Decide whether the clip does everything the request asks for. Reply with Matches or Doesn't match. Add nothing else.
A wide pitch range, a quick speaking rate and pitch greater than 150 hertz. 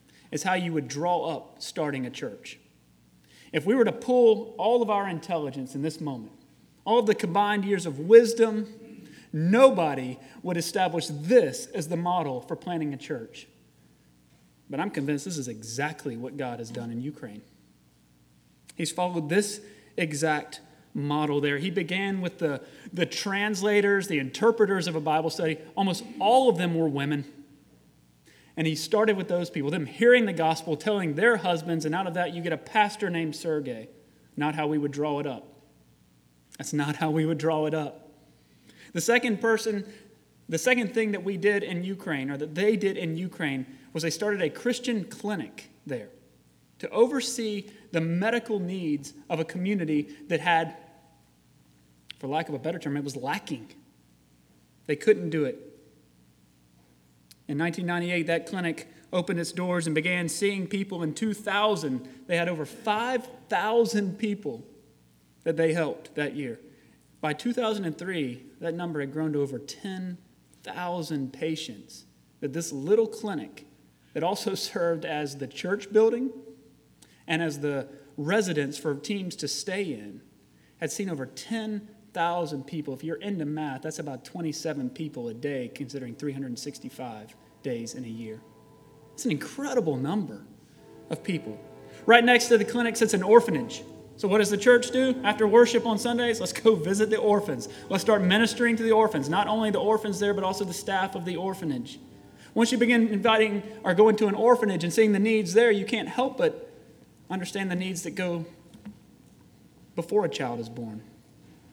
Doesn't match